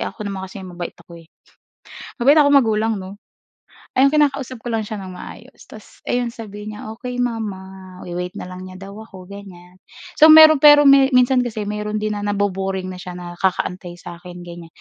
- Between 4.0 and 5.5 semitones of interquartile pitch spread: Yes, average, 4.8 semitones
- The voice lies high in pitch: Yes, high, 205 Hz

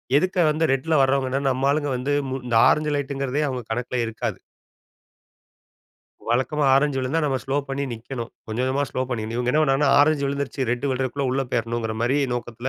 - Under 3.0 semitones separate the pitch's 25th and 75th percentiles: Yes, narrow, 2.5 semitones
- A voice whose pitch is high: No, low, 135 Hz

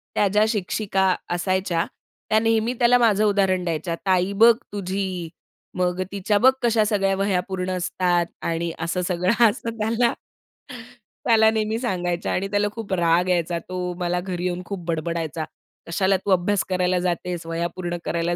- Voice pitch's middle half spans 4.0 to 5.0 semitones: No, average, 3.0 semitones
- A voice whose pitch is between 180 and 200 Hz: Yes, medium, 185 Hz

